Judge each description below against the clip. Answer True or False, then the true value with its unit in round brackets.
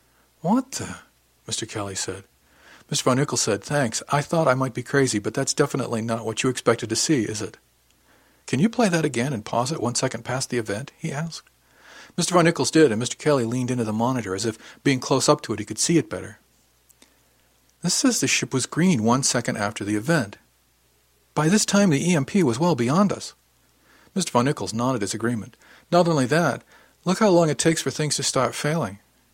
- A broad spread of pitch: True (5.9 semitones)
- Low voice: True (130 Hz)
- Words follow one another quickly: True (215 wpm)